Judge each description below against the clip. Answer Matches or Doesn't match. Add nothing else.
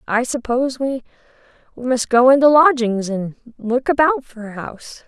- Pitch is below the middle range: Doesn't match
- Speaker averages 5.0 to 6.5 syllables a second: Doesn't match